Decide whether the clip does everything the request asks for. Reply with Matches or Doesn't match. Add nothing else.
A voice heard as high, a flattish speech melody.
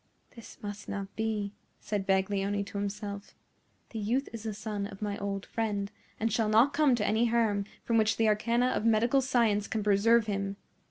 Matches